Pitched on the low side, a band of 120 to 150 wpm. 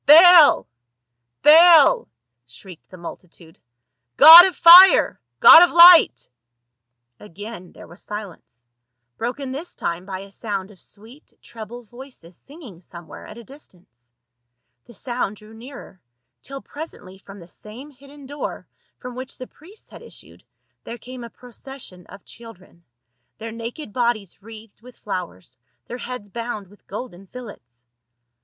No: high, 225 Hz; average, 145 wpm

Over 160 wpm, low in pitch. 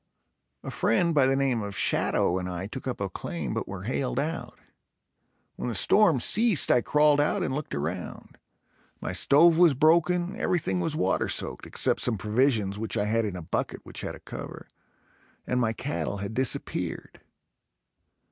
Yes: average, 175 wpm; low, 125 Hz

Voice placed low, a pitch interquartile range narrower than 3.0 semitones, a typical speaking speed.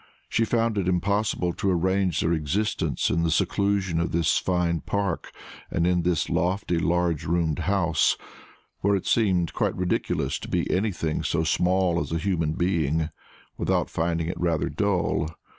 Yes: very low, 90 Hz; narrow, 2.6 semitones; average, 160 wpm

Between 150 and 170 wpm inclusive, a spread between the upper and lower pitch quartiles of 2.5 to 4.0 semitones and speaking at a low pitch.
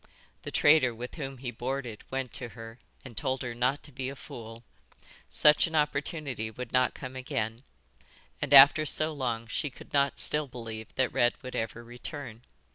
No: average, 180 wpm; average, 3.1 semitones; low, 130 Hz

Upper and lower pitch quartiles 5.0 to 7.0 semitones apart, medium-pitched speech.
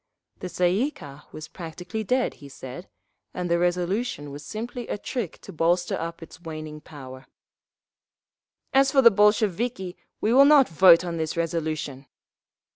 Yes: wide, 5.5 semitones; medium, 175 Hz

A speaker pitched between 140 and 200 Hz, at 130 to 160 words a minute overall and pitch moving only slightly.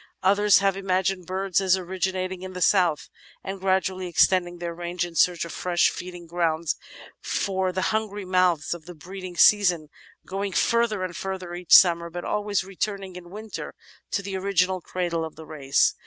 No: medium, 185 Hz; average, 170 wpm; narrow, 1.8 semitones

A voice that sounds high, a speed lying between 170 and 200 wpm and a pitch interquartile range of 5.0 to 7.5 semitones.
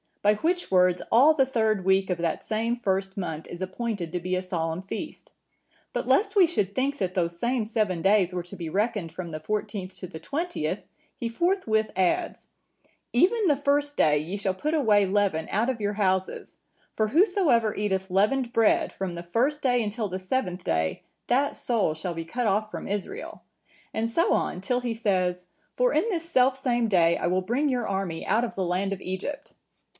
Yes: high, 205 Hz; average, 195 wpm; wide, 5.4 semitones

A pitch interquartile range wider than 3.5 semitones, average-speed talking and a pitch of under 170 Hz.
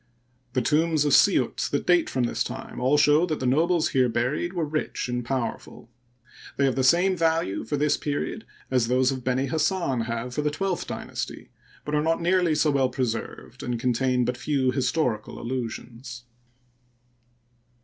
Yes: average, 3.9 semitones; average, 170 wpm; low, 135 Hz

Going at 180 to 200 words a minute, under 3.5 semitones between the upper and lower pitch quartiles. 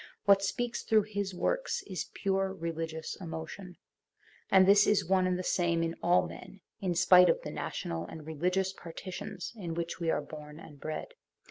Yes: average, 185 wpm; average, 2.8 semitones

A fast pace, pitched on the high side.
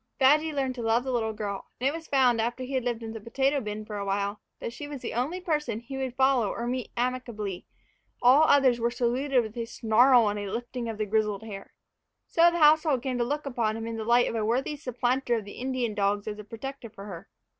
Yes: fast, 245 wpm; high, 240 Hz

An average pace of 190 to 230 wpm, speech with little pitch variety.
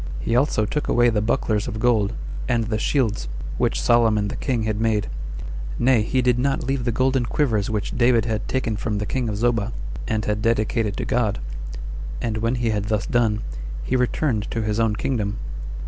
Yes: average, 195 wpm; narrow, 2.3 semitones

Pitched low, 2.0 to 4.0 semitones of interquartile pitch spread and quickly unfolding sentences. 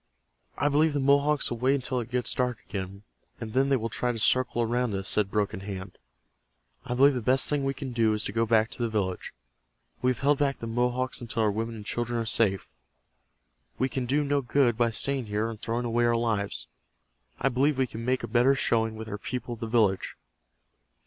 Yes: low, 120 Hz; average, 2.9 semitones; fast, 220 wpm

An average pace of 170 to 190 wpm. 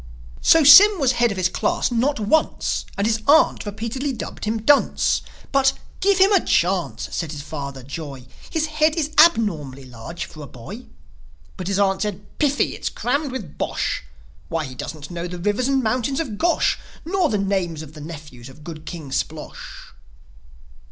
Yes: average, 180 wpm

